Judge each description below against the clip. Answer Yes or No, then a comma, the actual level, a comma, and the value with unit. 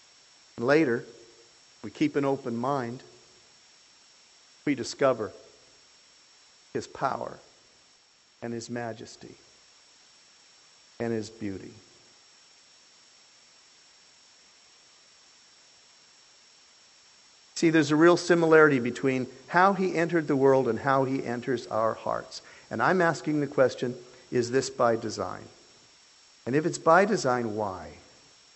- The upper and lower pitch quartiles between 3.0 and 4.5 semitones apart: No, average, 4.9 semitones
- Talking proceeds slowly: Yes, slow, 100 wpm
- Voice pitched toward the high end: No, low, 130 Hz